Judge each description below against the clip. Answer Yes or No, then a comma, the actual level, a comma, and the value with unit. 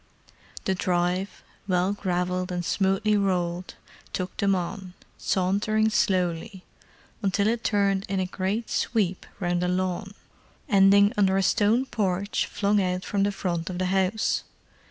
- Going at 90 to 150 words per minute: Yes, average, 140 wpm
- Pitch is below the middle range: No, high, 190 Hz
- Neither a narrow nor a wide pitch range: No, narrow, 1.9 semitones